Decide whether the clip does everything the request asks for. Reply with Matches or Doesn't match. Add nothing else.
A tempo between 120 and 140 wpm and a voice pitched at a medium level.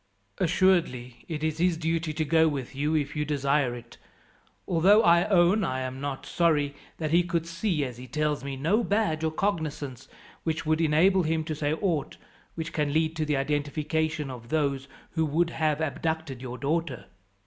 Doesn't match